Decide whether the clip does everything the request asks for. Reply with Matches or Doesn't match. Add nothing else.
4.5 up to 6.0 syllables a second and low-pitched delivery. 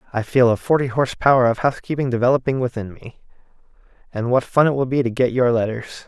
Doesn't match